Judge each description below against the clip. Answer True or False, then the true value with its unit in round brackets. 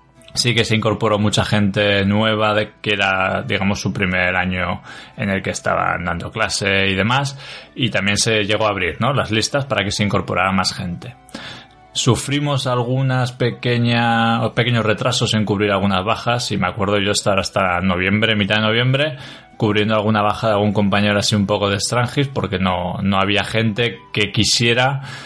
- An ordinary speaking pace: True (175 wpm)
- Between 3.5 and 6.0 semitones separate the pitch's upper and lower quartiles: False (3.0 semitones)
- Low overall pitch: True (105 Hz)